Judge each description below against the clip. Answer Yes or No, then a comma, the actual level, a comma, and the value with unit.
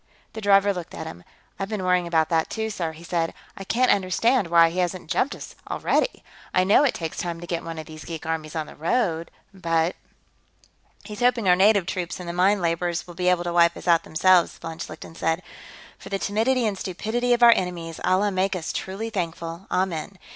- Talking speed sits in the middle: No, fast, 215 wpm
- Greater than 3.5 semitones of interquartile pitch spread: No, average, 3.2 semitones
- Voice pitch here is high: No, medium, 180 Hz